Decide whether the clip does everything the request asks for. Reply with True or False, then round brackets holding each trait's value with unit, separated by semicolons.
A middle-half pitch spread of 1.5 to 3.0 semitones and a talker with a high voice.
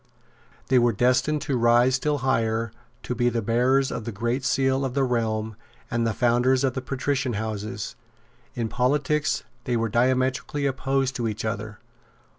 False (2.5 semitones; 125 Hz)